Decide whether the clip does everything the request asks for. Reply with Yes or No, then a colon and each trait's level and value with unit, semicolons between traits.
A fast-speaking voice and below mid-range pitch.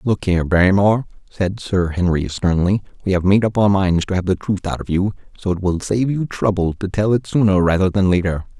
Yes: fast, 230 wpm; very low, 95 Hz